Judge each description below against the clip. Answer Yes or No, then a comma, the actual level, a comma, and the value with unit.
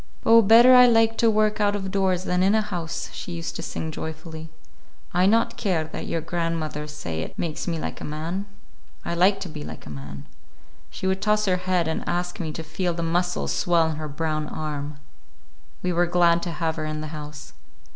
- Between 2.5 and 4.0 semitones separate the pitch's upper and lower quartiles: Yes, average, 3.4 semitones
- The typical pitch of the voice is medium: Yes, medium, 170 Hz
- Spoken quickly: Yes, fast, 215 wpm